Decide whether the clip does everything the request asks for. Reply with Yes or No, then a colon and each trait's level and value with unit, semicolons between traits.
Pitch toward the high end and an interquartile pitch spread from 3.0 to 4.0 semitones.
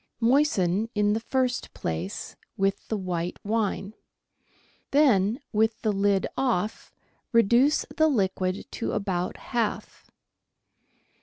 Yes: high, 210 Hz; average, 3.7 semitones